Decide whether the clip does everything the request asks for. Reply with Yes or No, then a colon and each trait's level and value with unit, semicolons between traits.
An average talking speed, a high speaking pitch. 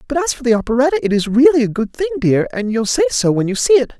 No: fast, 300 wpm; very high, 255 Hz